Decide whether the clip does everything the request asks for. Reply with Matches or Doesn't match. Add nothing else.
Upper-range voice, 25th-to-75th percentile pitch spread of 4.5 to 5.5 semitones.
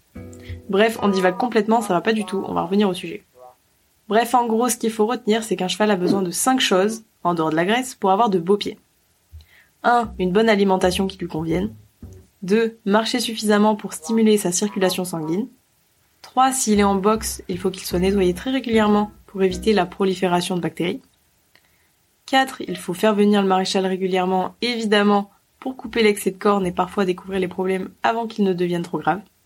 Doesn't match